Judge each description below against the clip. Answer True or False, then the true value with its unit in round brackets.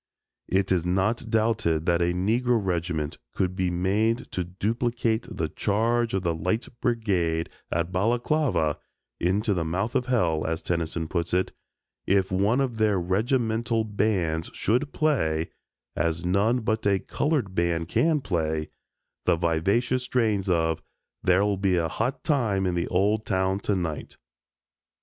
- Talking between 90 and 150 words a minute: True (145 wpm)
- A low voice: True (95 Hz)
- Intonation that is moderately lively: True (4.8 semitones)